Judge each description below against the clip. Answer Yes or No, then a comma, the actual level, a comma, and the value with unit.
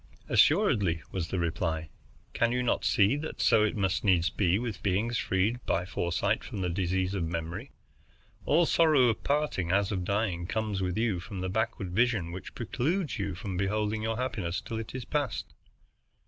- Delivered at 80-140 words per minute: No, average, 185 wpm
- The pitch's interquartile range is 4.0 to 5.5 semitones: Yes, average, 4.4 semitones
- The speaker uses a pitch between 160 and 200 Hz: No, low, 100 Hz